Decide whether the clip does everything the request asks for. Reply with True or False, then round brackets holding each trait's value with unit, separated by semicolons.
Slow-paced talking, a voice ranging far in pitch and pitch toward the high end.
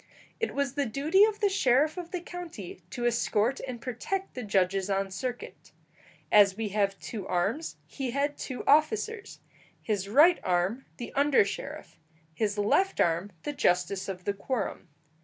False (160 wpm; 7.0 semitones; 240 Hz)